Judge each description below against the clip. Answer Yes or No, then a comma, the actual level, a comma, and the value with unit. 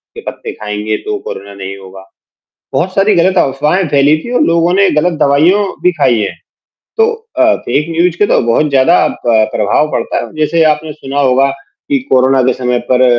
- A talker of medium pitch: Yes, medium, 145 Hz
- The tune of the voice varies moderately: No, wide, 5.9 semitones